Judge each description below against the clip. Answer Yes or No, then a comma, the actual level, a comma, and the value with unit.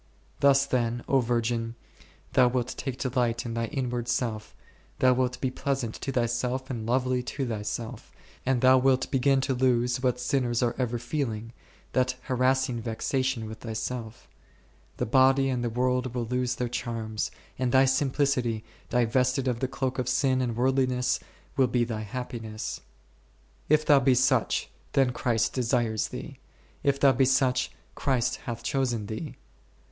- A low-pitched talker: Yes, low, 125 Hz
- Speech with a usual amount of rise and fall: No, narrow, 1.9 semitones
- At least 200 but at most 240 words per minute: No, average, 160 wpm